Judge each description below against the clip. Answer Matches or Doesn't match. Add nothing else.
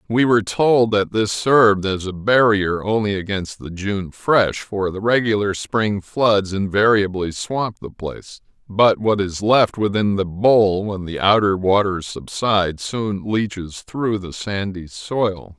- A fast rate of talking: Doesn't match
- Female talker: Doesn't match